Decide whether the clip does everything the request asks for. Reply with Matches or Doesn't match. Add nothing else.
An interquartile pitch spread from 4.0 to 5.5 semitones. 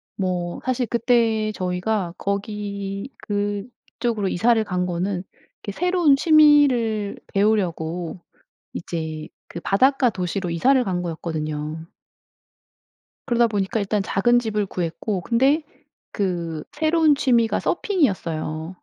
Matches